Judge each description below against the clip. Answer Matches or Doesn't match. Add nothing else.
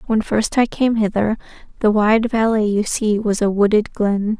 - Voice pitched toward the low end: Doesn't match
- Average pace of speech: Matches